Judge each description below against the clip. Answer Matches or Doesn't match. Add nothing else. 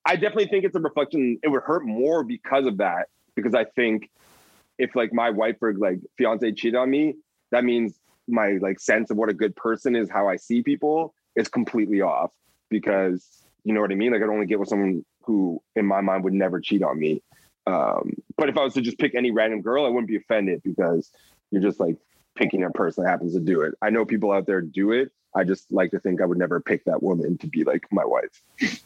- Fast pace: Matches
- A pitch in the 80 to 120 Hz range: Matches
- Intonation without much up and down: Doesn't match